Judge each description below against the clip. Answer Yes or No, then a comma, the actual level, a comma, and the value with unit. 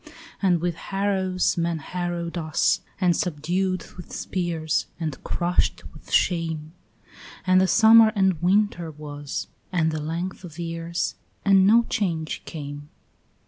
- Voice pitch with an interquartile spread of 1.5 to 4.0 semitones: Yes, average, 2.8 semitones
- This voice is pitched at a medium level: Yes, medium, 175 Hz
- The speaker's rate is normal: No, slow, 130 wpm